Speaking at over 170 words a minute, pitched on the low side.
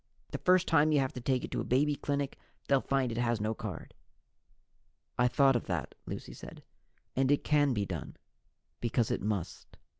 Yes: average, 190 wpm; low, 130 Hz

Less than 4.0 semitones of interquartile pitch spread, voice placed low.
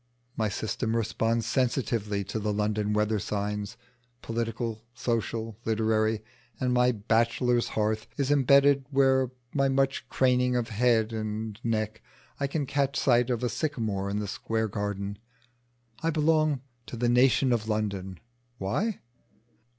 Yes: average, 3.1 semitones; low, 115 Hz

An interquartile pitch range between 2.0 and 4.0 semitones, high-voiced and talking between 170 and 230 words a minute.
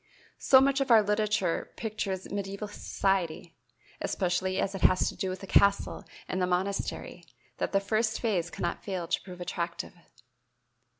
No: narrow, 2.6 semitones; high, 195 Hz; average, 160 wpm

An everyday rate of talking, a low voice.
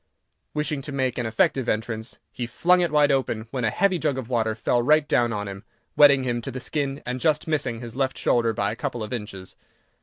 No: fast, 230 wpm; low, 125 Hz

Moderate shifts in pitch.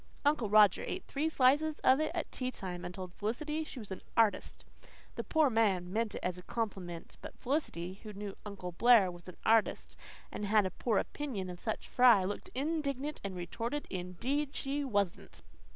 No: wide, 6.7 semitones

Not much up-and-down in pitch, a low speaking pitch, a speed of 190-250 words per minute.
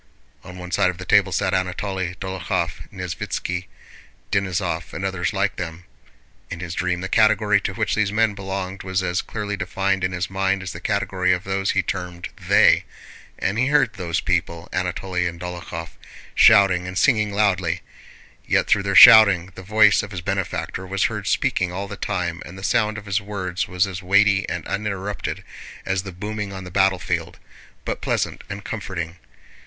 No: narrow, 1.8 semitones; very low, 95 Hz; average, 180 wpm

